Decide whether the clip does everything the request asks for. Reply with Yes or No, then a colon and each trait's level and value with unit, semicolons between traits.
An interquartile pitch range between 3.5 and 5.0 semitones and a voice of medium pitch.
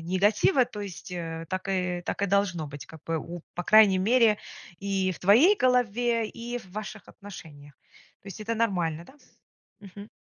No: average, 3.8 semitones; high, 200 Hz